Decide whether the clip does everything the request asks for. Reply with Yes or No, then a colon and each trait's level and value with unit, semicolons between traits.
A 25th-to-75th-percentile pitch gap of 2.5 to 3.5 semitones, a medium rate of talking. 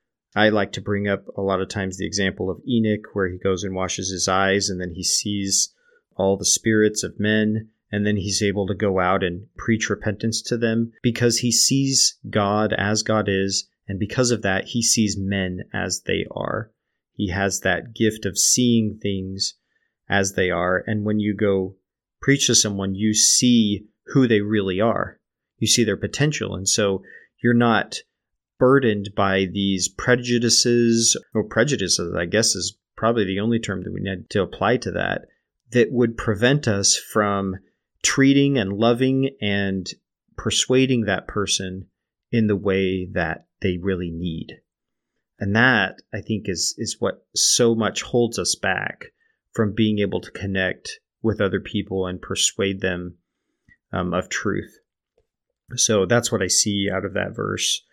Yes: average, 3.0 semitones; average, 170 wpm